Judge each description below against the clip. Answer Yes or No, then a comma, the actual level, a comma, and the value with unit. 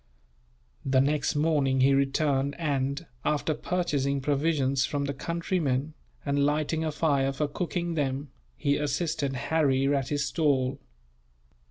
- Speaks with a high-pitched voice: No, medium, 145 Hz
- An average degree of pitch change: No, narrow, 2.2 semitones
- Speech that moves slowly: Yes, slow, 130 wpm